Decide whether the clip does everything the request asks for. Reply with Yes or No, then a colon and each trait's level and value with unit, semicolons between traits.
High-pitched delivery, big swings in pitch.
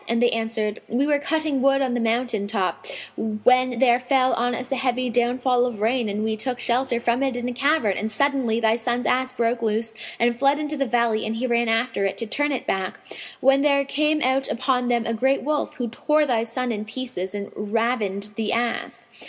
No: high, 245 Hz; average, 2.7 semitones